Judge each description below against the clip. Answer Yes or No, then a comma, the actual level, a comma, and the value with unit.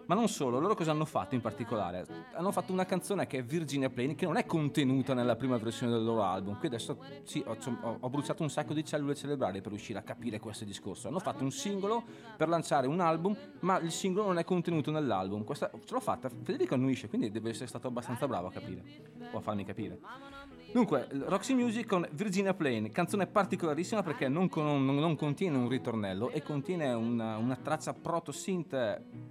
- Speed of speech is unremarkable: No, fast, 200 wpm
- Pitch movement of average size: No, wide, 7.2 semitones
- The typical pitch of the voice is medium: Yes, medium, 145 Hz